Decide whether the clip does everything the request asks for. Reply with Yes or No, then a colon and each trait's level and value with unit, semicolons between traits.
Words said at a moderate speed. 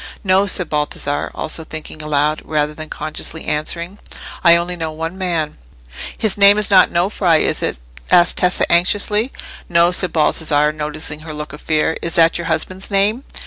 Yes: average, 170 wpm